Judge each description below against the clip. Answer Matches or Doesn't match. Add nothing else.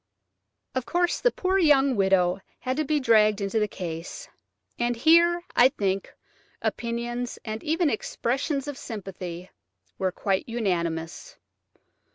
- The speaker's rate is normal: Doesn't match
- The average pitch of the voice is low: Doesn't match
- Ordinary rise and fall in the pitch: Doesn't match